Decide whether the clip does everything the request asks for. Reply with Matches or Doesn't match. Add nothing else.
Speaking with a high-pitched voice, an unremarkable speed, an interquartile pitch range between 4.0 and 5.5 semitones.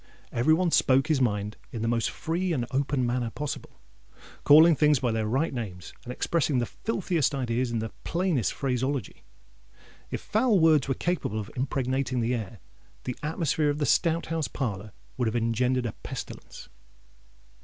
Doesn't match